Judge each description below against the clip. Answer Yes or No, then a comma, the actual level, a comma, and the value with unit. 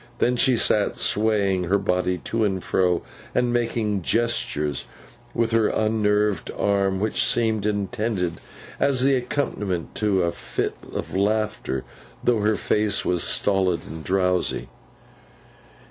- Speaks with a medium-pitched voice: No, low, 105 Hz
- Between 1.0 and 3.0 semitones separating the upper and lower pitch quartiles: No, average, 3.4 semitones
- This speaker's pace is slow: Yes, slow, 130 wpm